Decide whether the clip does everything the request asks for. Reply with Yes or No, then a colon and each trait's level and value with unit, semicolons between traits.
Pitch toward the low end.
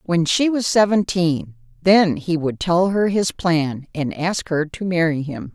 No: medium, 170 Hz